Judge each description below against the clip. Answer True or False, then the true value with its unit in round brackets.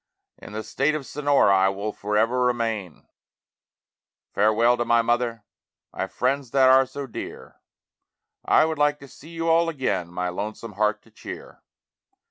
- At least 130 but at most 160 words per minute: True (155 wpm)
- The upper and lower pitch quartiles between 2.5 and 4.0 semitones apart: False (4.7 semitones)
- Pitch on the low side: True (120 Hz)